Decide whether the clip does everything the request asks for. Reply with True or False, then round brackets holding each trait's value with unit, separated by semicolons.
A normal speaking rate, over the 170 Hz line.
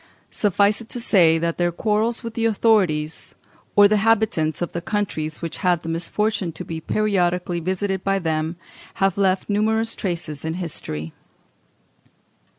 True (155 wpm; 185 Hz)